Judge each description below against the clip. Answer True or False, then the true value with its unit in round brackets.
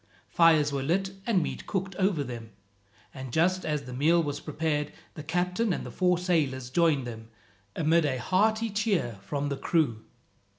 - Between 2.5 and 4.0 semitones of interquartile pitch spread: False (4.8 semitones)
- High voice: False (160 Hz)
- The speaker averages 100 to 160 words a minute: False (170 wpm)